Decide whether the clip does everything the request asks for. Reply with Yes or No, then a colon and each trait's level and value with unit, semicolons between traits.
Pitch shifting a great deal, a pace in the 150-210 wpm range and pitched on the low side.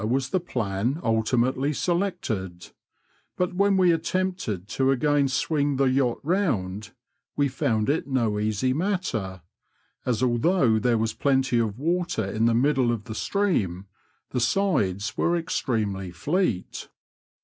No: wide, 7.0 semitones; slow, 135 wpm; low, 130 Hz